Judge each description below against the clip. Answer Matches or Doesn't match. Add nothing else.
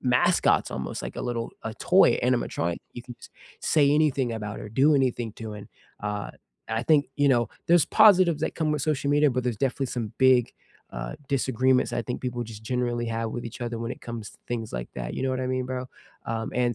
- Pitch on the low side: Matches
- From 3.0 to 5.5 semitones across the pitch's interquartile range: Doesn't match